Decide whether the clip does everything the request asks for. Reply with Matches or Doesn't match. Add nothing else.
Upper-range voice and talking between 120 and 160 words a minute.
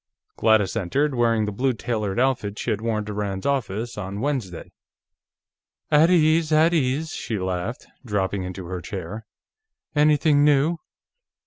Doesn't match